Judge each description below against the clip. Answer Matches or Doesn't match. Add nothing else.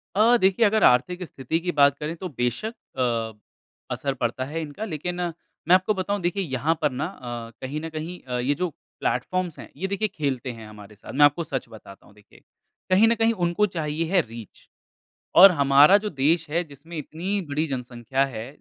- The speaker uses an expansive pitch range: Matches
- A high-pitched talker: Doesn't match